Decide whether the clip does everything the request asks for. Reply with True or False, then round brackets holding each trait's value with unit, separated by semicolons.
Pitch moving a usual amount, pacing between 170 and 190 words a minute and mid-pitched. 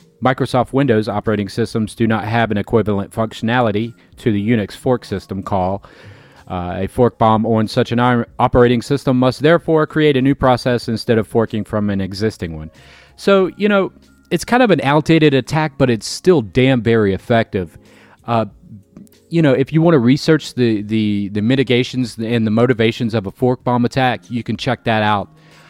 False (3.7 semitones; 185 wpm; 120 Hz)